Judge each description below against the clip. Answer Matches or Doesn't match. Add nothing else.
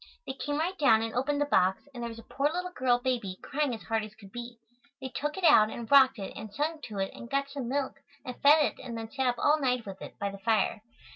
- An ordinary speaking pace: Doesn't match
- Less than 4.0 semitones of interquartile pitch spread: Doesn't match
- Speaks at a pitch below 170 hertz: Doesn't match